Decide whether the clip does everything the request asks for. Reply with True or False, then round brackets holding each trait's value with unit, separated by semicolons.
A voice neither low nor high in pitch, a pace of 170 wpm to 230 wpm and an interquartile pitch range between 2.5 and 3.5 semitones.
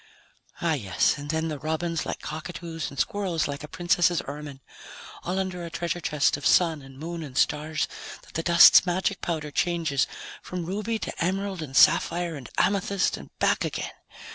True (165 Hz; 175 wpm; 2.9 semitones)